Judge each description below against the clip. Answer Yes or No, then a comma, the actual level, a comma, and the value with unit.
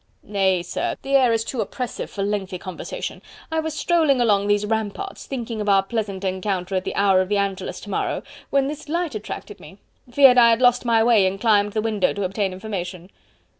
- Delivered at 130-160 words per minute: No, fast, 205 wpm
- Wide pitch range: No, average, 3.8 semitones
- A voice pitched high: Yes, high, 210 Hz